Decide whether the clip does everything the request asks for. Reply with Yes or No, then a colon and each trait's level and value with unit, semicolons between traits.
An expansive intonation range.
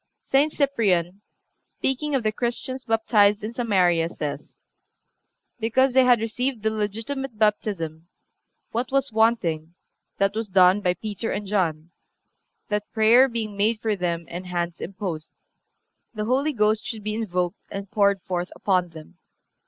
No: average, 4.3 semitones